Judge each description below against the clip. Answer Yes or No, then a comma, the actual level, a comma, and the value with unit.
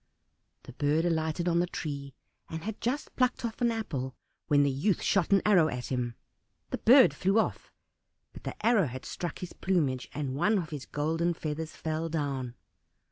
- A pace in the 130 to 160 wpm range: No, average, 185 wpm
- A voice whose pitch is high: No, medium, 160 Hz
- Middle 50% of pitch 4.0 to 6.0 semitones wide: Yes, wide, 5.5 semitones